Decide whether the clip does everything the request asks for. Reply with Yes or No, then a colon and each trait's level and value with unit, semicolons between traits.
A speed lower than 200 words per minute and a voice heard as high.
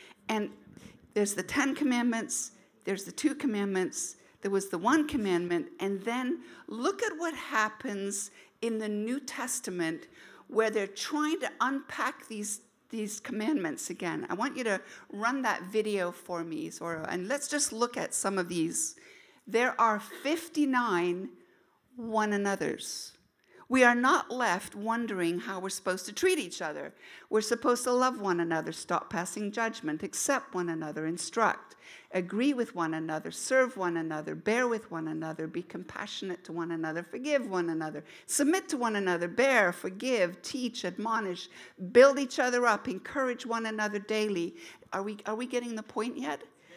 Yes: average, 160 wpm; high, 220 Hz